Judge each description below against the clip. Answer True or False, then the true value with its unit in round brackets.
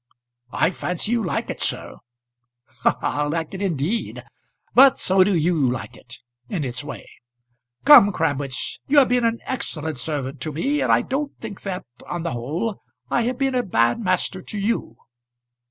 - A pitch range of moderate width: False (7.9 semitones)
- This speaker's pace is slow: False (175 wpm)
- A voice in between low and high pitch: True (180 Hz)